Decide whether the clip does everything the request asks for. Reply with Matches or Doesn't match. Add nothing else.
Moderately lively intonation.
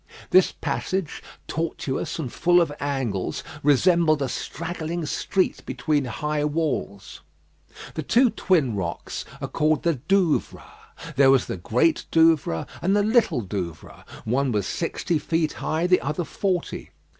Matches